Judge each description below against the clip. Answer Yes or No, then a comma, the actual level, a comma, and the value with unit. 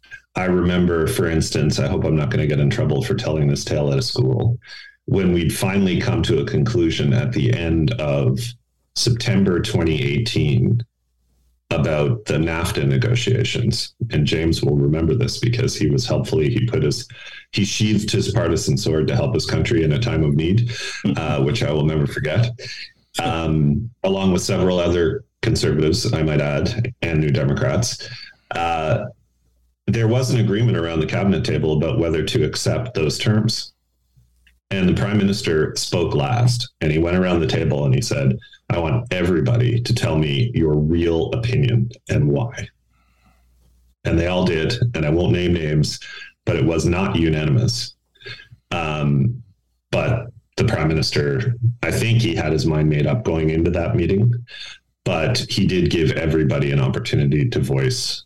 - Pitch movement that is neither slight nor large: No, wide, 7.8 semitones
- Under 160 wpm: No, average, 165 wpm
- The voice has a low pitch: Yes, very low, 90 Hz